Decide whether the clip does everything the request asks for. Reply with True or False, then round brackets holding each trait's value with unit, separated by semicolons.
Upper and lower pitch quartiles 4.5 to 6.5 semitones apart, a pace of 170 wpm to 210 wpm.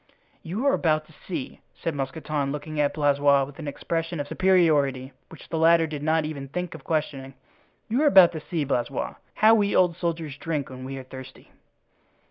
False (3.2 semitones; 190 wpm)